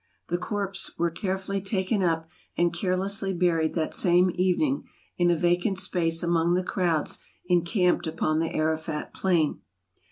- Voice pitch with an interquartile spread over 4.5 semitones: No, narrow, 2.5 semitones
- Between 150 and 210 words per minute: No, average, 140 wpm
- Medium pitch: Yes, medium, 175 Hz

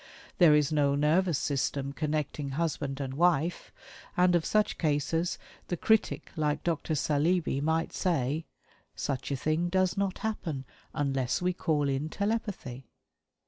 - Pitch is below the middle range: No, medium, 155 Hz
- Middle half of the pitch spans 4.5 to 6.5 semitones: No, average, 3.8 semitones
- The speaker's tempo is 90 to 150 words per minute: Yes, average, 140 wpm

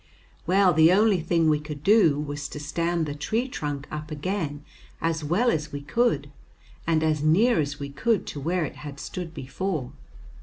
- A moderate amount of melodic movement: Yes, average, 3.7 semitones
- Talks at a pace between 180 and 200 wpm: Yes, average, 185 wpm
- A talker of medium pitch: Yes, medium, 155 Hz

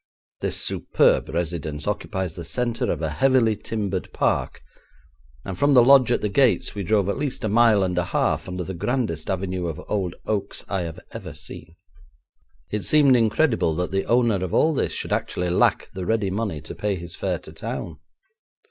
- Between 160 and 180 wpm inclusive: No, average, 190 wpm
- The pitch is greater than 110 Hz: No, low, 100 Hz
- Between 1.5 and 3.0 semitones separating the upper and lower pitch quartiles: No, average, 4.8 semitones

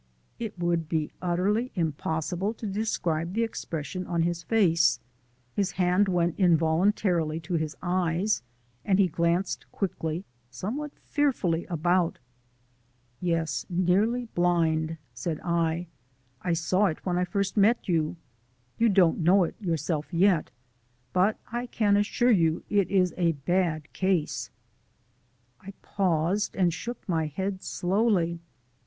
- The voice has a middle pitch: Yes, medium, 180 Hz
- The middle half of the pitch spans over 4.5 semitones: No, average, 3.3 semitones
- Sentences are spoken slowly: Yes, slow, 130 wpm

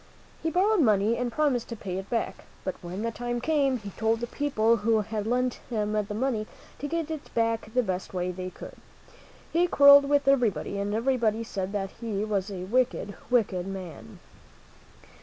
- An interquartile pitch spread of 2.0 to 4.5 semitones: Yes, average, 4.1 semitones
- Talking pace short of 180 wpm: No, average, 185 wpm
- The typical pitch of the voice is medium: No, high, 225 Hz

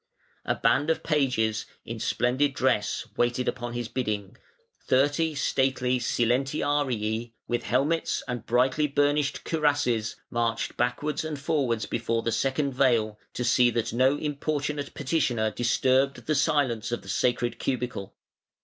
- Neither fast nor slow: No, slow, 130 wpm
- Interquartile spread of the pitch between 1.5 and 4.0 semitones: Yes, average, 3.4 semitones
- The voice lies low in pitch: Yes, low, 125 Hz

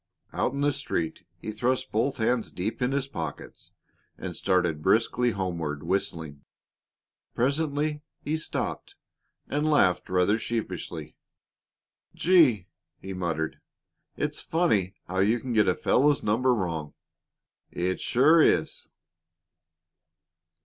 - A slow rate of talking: Yes, slow, 115 wpm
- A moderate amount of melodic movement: No, wide, 7.5 semitones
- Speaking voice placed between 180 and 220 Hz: No, low, 110 Hz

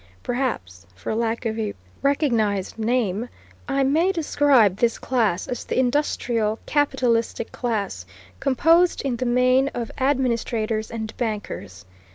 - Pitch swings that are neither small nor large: Yes, average, 3.4 semitones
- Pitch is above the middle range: Yes, high, 235 Hz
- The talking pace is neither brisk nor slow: No, slow, 125 wpm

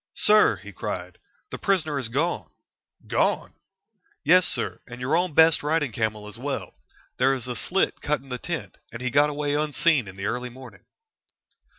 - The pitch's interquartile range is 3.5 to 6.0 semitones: Yes, average, 4.6 semitones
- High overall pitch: No, medium, 140 Hz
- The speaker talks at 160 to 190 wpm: Yes, average, 180 wpm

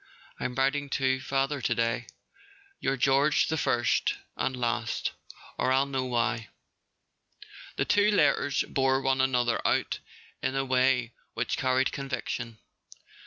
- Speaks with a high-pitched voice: No, low, 130 Hz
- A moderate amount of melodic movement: No, narrow, 1.8 semitones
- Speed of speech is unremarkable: No, slow, 125 wpm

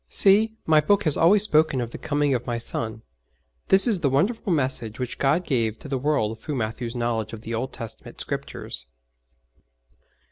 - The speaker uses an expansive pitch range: Yes, wide, 5.7 semitones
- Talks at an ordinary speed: Yes, average, 180 wpm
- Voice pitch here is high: No, low, 135 Hz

